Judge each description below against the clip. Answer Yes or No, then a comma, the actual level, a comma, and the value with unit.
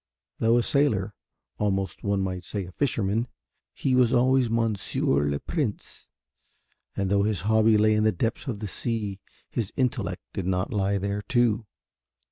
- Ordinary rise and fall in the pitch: Yes, average, 3.2 semitones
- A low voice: Yes, low, 105 Hz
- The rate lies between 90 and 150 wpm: No, average, 160 wpm